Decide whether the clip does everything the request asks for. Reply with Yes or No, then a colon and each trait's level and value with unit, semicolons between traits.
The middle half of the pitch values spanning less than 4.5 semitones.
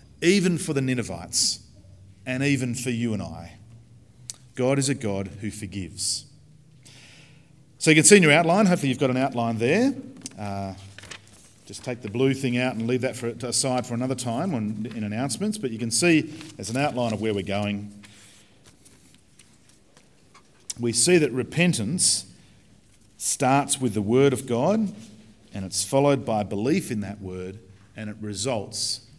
No: average, 4.8 semitones